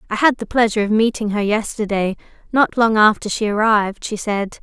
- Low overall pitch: No, high, 215 Hz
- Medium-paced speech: Yes, average, 195 wpm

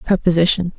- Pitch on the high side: No, medium, 175 Hz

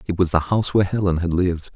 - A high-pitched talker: No, very low, 90 Hz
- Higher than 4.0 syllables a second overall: Yes, 7.5 syllables/s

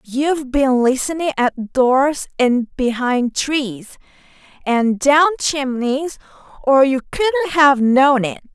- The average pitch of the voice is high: Yes, very high, 270 Hz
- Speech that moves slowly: Yes, slow, 100 wpm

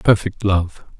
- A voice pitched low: Yes, low, 100 Hz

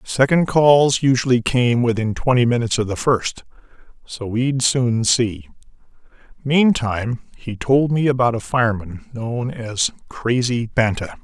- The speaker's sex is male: Yes, male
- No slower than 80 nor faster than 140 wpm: Yes, slow, 135 wpm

